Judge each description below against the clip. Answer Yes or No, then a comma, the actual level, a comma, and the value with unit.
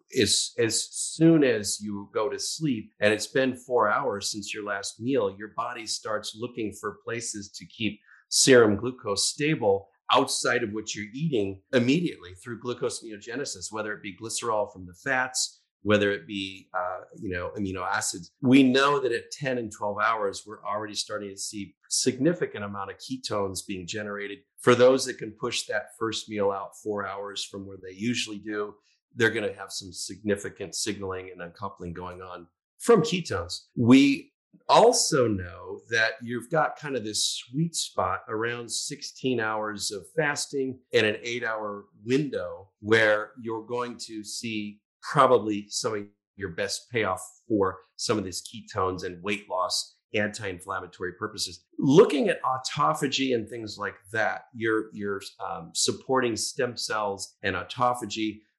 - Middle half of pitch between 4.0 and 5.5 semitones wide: No, average, 3.6 semitones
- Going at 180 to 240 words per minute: No, average, 165 wpm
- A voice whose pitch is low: Yes, low, 105 Hz